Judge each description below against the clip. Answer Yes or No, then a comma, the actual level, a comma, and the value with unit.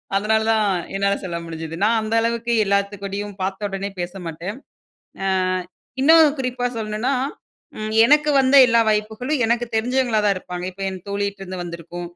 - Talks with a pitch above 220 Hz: No, high, 210 Hz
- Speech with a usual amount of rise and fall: Yes, average, 3.3 semitones